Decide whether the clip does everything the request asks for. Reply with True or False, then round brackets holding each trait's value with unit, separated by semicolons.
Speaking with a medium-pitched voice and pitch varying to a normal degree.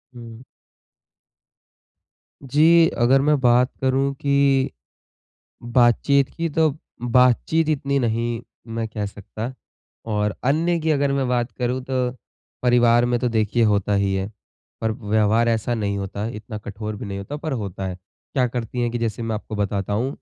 False (120 Hz; 3.8 semitones)